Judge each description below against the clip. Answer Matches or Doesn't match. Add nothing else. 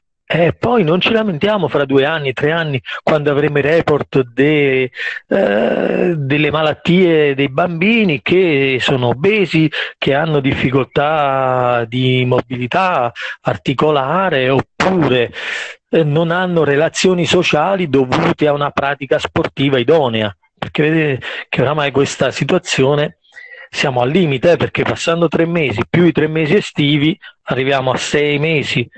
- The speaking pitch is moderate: Matches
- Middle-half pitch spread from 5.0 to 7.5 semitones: Doesn't match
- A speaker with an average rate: Matches